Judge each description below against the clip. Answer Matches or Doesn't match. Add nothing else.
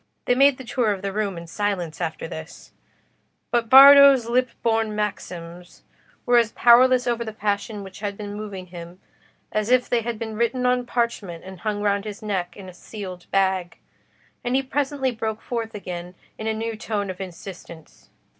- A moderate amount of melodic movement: Matches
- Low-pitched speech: Doesn't match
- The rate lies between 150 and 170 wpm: Doesn't match